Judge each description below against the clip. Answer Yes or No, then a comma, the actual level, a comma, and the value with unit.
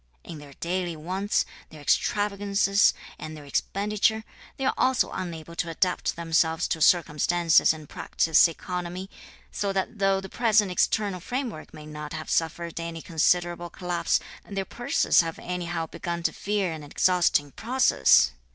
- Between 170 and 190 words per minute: No, average, 145 wpm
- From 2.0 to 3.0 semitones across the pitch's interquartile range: No, average, 3.4 semitones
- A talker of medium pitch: Yes, medium, 175 Hz